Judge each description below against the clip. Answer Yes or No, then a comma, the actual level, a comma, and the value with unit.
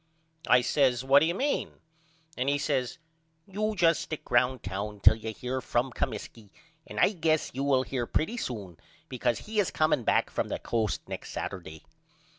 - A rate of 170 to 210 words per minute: Yes, average, 180 wpm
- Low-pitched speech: Yes, low, 130 Hz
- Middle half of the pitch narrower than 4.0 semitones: No, wide, 5.6 semitones